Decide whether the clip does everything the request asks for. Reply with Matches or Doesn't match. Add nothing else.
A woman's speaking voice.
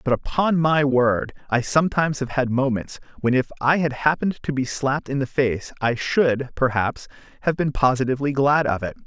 Doesn't match